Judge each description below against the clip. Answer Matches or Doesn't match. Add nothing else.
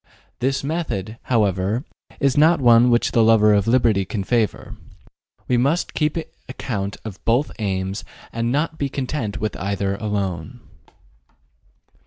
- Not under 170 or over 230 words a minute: Doesn't match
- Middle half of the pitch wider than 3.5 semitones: Matches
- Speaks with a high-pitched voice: Doesn't match